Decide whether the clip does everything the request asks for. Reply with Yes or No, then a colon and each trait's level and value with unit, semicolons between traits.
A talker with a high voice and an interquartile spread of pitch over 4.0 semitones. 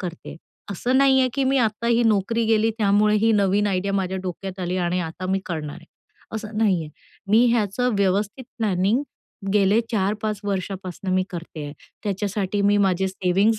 No: high, 200 Hz; average, 2.8 semitones